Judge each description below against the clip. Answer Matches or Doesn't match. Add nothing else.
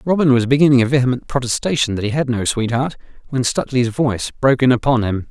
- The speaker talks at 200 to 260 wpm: Matches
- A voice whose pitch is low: Matches